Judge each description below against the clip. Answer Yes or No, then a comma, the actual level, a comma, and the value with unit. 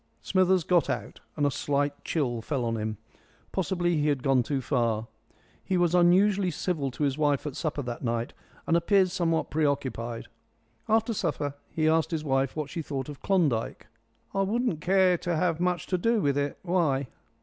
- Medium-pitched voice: Yes, medium, 155 Hz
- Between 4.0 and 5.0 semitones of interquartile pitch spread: Yes, average, 4.7 semitones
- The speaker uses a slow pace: No, average, 185 wpm